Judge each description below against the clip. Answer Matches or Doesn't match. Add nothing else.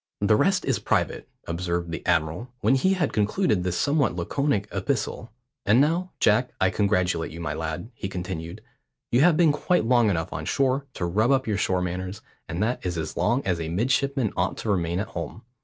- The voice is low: Matches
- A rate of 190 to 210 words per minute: Matches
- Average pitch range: Doesn't match